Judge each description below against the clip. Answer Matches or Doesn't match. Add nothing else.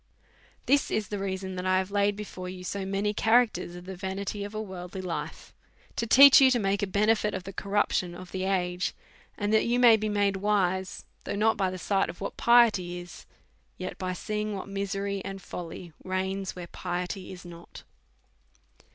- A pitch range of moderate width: Doesn't match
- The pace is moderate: Matches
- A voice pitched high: Matches